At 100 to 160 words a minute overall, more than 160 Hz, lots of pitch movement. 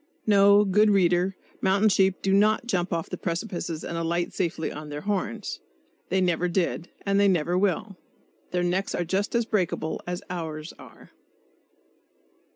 No: average, 155 wpm; medium, 185 Hz; average, 2.7 semitones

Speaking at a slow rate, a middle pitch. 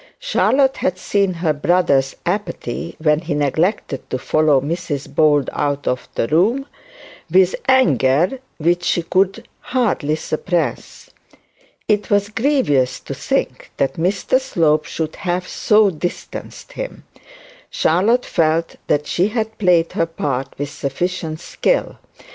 Yes: slow, 130 wpm; medium, 170 Hz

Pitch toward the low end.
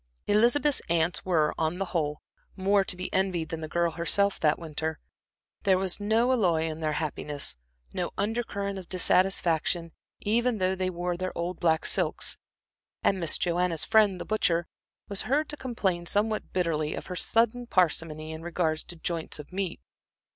No: medium, 180 Hz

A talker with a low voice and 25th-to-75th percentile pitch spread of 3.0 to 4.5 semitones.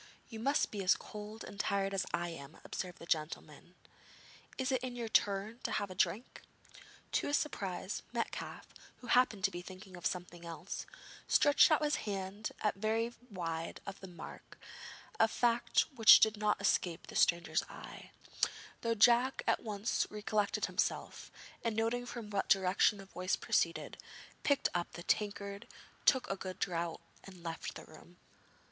No: high, 200 Hz; average, 3.8 semitones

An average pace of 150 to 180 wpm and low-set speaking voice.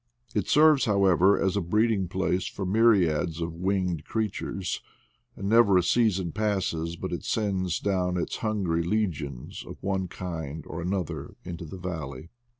Yes: average, 155 wpm; very low, 95 Hz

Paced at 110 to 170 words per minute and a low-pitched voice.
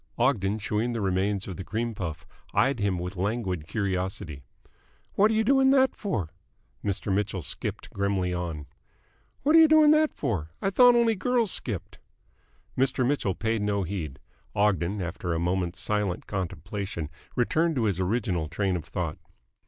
Yes: average, 160 wpm; low, 100 Hz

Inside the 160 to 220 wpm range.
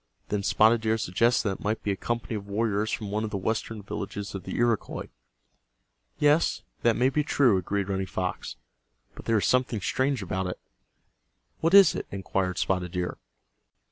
Yes: average, 180 wpm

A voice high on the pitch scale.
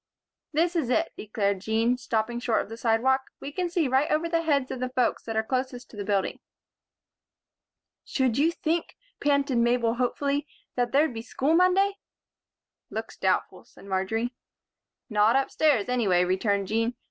Yes: very high, 250 Hz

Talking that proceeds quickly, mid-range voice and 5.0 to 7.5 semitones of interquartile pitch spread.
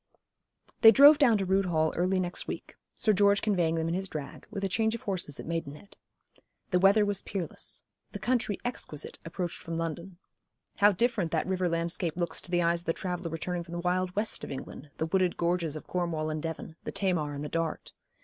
No: fast, 210 wpm; medium, 180 Hz; average, 3.0 semitones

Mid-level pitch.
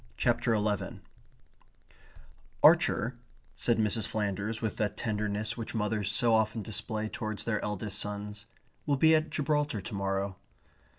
No: low, 110 Hz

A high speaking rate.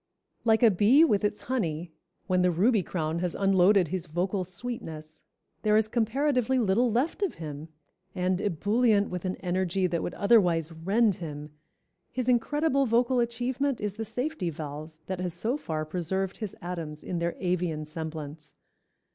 No: average, 165 wpm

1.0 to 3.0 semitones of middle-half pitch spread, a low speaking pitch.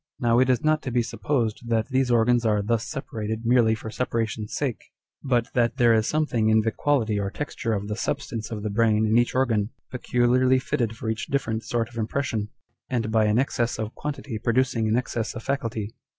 Yes: narrow, 2.5 semitones; low, 115 Hz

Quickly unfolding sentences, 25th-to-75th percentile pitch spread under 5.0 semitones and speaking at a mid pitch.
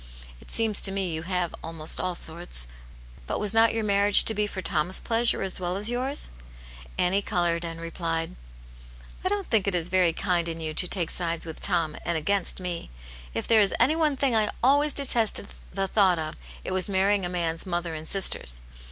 Yes: fast, 215 wpm; average, 4.1 semitones; medium, 180 Hz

